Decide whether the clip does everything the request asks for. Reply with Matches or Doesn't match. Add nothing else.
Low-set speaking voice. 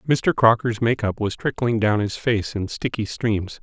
Matches